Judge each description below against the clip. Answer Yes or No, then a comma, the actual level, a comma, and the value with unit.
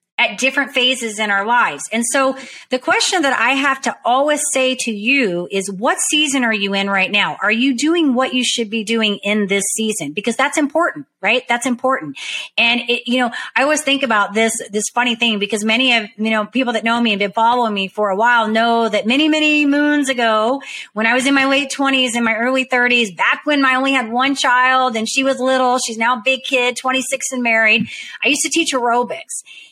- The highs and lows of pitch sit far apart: No, average, 3.3 semitones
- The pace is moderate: No, fast, 225 wpm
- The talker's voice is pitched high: Yes, very high, 250 Hz